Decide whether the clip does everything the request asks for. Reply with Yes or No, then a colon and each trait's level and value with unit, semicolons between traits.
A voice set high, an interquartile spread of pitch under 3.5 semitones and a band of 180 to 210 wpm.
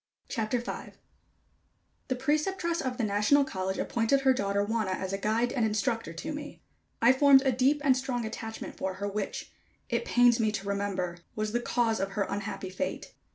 No: high, 225 Hz; average, 4.5 semitones; average, 185 wpm